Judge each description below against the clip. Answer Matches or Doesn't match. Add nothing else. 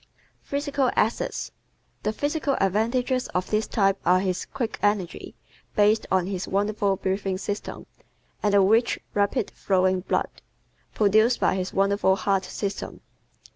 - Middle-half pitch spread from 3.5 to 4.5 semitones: Doesn't match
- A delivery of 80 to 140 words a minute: Matches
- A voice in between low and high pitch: Doesn't match